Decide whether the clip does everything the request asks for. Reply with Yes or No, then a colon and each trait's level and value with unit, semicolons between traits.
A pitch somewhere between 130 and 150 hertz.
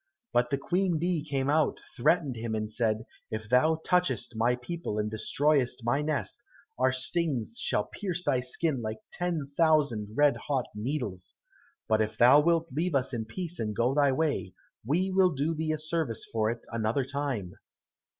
Yes: low, 135 Hz